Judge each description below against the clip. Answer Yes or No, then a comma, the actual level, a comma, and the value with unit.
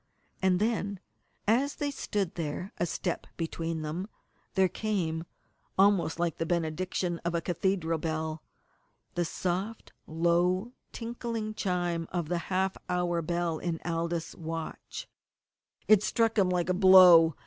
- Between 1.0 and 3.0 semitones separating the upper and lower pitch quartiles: Yes, narrow, 2.6 semitones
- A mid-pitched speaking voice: Yes, medium, 175 Hz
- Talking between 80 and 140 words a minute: Yes, slow, 135 wpm